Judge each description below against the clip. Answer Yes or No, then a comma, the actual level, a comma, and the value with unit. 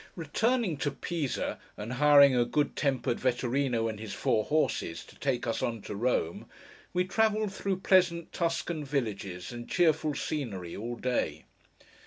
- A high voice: No, medium, 140 Hz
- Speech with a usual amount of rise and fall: No, wide, 6.2 semitones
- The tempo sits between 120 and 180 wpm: Yes, average, 150 wpm